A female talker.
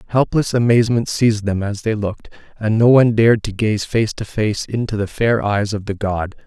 No: male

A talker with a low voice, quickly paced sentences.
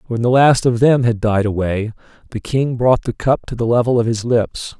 Yes: low, 120 Hz; fast, 240 wpm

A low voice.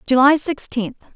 No: very high, 270 Hz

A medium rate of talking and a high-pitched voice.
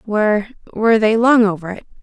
Yes: average, 150 wpm; high, 215 Hz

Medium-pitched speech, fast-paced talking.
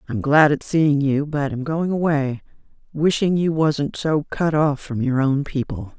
No: medium, 145 Hz; average, 190 wpm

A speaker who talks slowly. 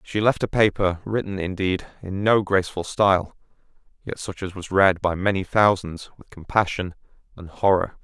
No: average, 165 wpm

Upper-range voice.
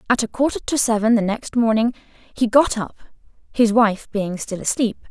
Yes: high, 225 Hz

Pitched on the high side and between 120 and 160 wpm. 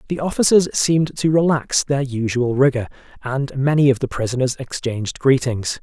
No: low, 135 Hz; average, 155 wpm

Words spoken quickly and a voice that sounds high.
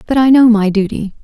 Yes: fast, 245 wpm; high, 225 Hz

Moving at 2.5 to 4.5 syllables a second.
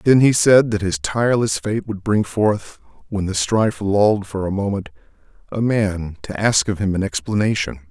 No: 5.0 syllables/s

